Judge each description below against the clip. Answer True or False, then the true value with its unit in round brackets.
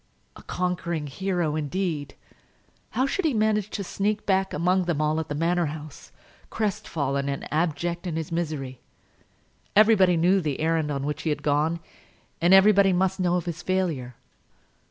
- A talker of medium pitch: True (170 Hz)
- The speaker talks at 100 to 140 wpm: False (160 wpm)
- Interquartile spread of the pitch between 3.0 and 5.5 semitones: True (4.0 semitones)